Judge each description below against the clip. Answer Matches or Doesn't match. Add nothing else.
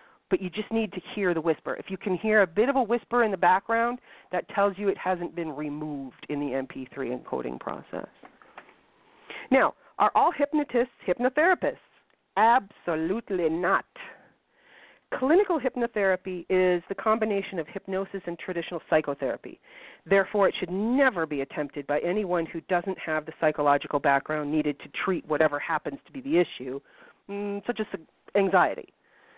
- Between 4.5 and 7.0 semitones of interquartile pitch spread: Matches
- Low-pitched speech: Doesn't match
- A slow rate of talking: Doesn't match